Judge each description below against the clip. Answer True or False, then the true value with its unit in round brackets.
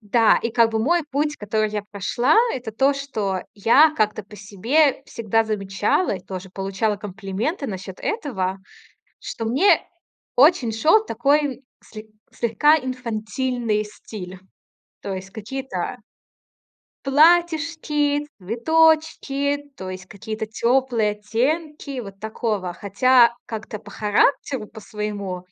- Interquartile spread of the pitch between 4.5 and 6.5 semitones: True (5.1 semitones)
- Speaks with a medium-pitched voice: False (225 Hz)